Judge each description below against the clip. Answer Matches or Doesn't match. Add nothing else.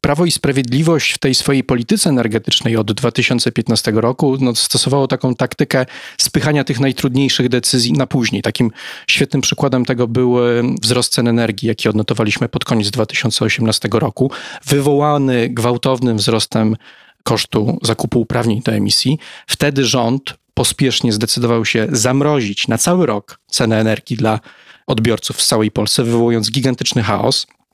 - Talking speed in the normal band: Matches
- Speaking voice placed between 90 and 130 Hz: Matches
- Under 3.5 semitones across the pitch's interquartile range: Matches